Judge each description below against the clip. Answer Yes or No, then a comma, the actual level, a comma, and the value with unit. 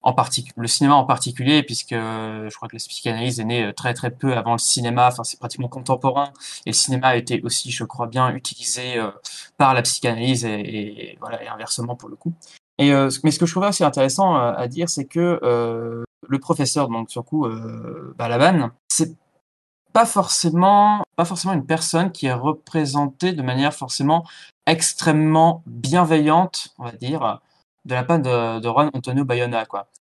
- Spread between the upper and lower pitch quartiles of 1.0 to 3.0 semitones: No, average, 4.9 semitones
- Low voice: Yes, low, 130 Hz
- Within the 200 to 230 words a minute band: No, average, 180 wpm